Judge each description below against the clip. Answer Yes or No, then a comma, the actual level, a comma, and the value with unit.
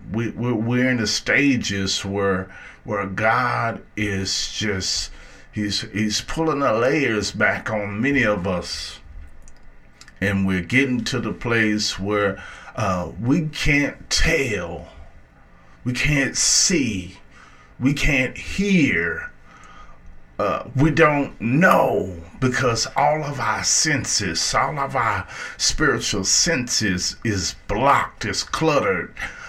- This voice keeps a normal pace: No, slow, 110 wpm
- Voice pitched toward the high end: No, low, 105 Hz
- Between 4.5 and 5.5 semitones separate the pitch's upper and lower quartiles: Yes, average, 5.1 semitones